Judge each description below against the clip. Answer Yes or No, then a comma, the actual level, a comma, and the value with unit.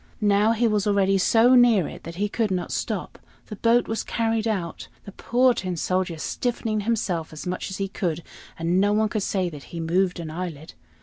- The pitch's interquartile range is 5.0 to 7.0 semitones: No, average, 4.2 semitones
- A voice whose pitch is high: Yes, high, 195 Hz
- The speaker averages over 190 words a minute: Yes, fast, 205 wpm